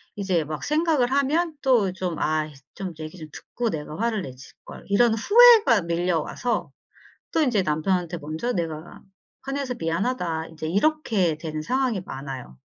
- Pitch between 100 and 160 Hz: No, medium, 185 Hz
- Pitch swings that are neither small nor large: No, wide, 7.9 semitones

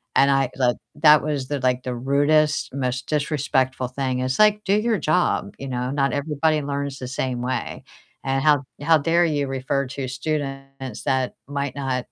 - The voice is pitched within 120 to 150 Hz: Yes, medium, 140 Hz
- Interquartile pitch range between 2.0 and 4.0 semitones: Yes, narrow, 2.4 semitones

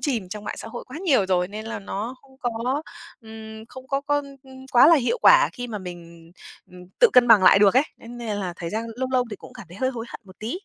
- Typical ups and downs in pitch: Yes, average, 4.7 semitones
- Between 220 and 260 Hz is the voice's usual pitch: Yes, high, 225 Hz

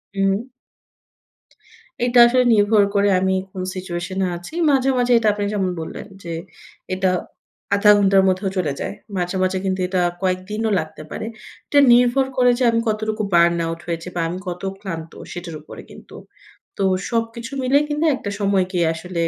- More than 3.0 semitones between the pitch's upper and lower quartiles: Yes, average, 4.1 semitones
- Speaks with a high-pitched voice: Yes, high, 195 Hz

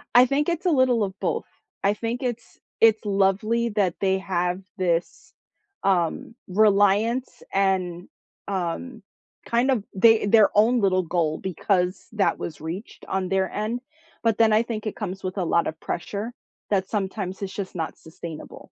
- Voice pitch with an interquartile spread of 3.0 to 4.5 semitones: Yes, average, 3.5 semitones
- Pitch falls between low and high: No, high, 200 Hz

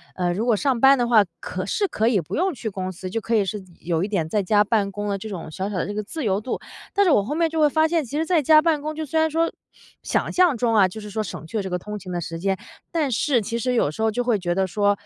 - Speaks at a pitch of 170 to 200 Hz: No, high, 215 Hz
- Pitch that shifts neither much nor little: No, wide, 7.0 semitones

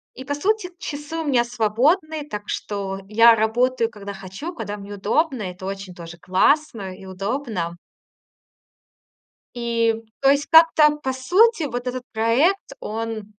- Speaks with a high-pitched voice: Yes, high, 235 Hz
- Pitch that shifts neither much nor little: No, wide, 6.3 semitones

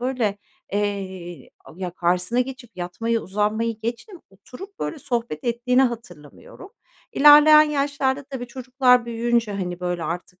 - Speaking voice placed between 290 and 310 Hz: No, high, 235 Hz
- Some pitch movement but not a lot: No, wide, 5.7 semitones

